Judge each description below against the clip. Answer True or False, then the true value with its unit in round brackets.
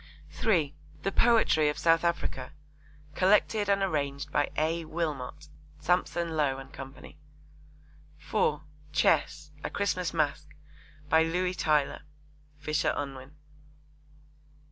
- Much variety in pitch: False (2.9 semitones)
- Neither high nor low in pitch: True (155 Hz)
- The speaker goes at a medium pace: False (105 wpm)